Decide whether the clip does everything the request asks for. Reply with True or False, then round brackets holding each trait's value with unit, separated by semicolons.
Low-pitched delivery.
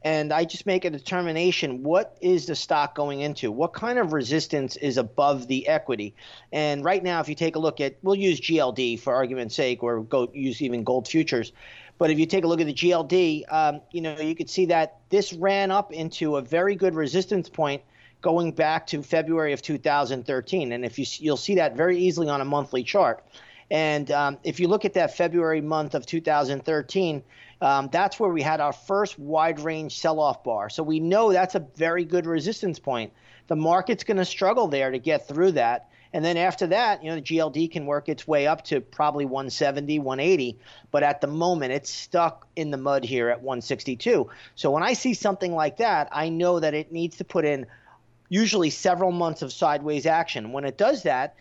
False (155 Hz)